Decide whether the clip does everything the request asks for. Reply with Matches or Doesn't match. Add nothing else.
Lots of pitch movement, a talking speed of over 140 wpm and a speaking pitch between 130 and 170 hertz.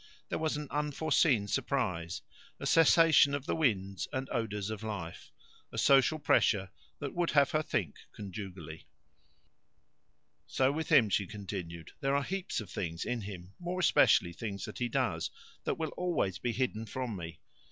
Doesn't match